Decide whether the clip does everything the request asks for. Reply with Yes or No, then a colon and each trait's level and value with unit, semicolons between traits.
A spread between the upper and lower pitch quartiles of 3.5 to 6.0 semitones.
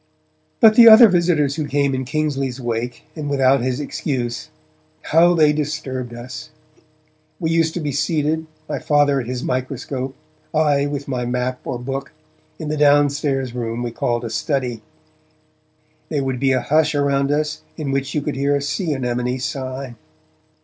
No: average, 2.8 semitones